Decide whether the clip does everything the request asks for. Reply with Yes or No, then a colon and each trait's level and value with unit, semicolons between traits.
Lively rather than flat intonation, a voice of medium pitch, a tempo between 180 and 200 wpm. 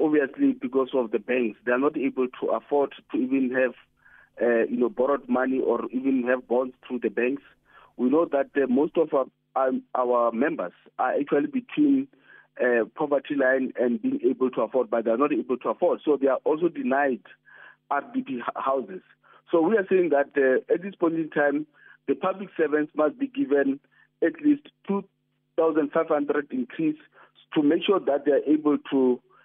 Yes: wide, 6.2 semitones; medium, 145 Hz; average, 190 wpm